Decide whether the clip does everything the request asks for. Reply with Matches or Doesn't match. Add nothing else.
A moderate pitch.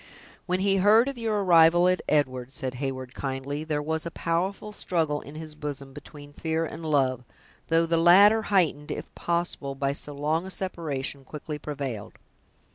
Matches